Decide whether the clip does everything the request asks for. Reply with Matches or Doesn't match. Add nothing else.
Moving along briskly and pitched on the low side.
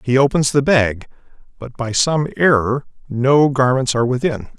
Doesn't match